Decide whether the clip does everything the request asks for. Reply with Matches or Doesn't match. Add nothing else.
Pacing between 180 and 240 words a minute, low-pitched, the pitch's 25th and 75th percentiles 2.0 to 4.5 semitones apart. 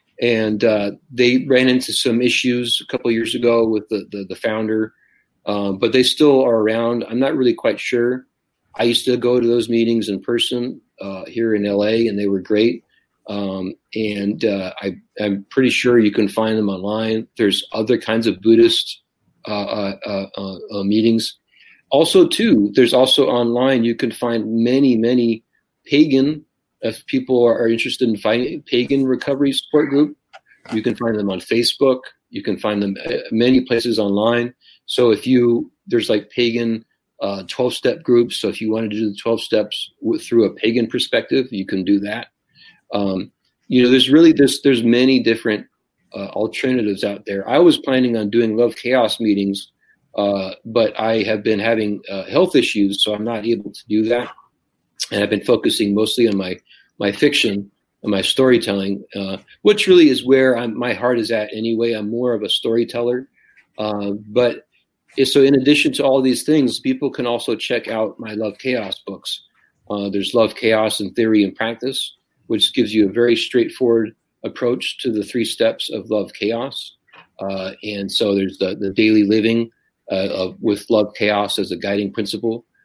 Matches